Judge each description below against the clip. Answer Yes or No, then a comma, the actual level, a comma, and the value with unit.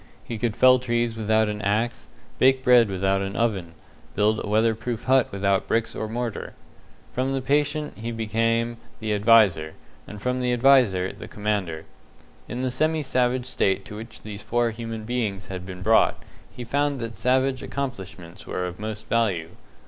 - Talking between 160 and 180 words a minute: Yes, average, 170 wpm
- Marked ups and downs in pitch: No, average, 3.4 semitones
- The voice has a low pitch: Yes, low, 115 Hz